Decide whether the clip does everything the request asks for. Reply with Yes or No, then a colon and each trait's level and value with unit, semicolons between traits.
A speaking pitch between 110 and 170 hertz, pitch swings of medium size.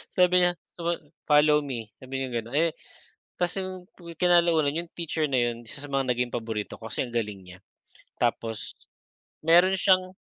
No: medium, 140 Hz; wide, 6.6 semitones